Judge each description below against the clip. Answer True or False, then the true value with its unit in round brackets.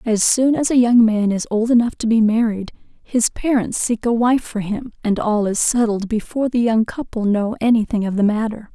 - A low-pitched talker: False (225 Hz)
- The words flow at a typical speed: False (225 wpm)